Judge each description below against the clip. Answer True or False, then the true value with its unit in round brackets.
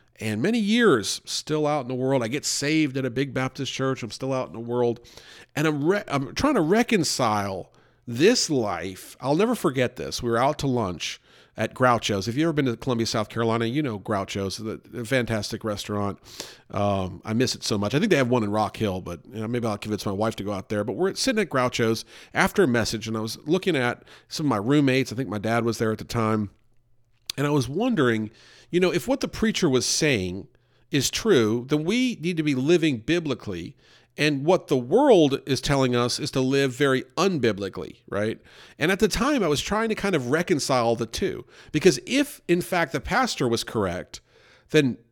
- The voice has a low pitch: True (130 Hz)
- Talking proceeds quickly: True (220 wpm)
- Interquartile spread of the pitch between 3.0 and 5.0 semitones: False (5.5 semitones)